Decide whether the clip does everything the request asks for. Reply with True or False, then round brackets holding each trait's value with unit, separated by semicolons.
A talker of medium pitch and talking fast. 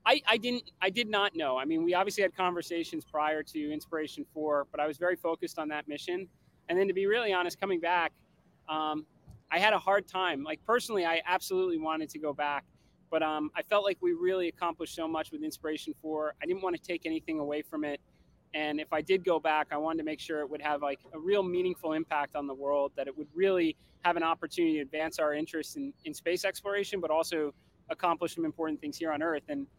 True (165 Hz; 235 wpm)